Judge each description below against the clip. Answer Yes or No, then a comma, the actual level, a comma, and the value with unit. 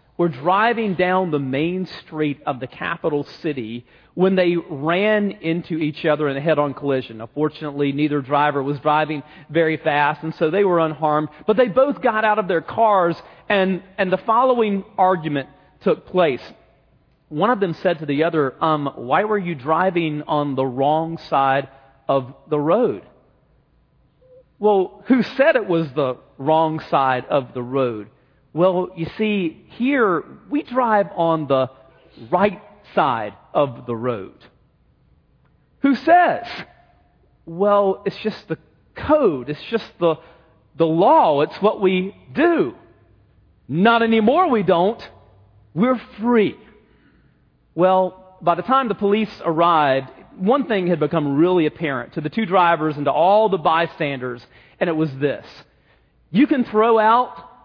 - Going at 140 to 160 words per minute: Yes, average, 150 wpm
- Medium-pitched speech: Yes, medium, 165 Hz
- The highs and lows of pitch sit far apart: Yes, wide, 5.7 semitones